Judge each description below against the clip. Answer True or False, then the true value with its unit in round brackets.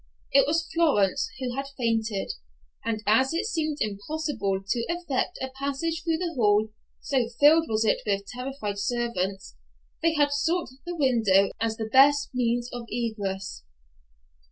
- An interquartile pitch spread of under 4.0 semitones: False (5.4 semitones)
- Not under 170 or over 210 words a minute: False (150 wpm)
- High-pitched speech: True (245 Hz)